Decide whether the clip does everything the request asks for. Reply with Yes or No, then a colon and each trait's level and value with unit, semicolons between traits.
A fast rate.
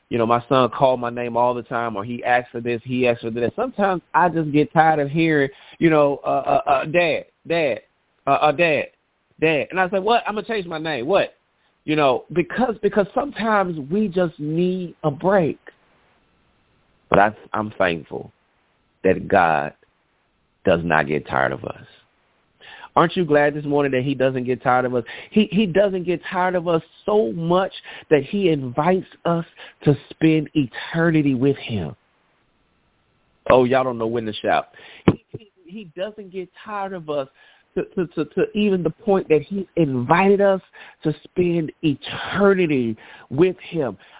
No: average, 180 wpm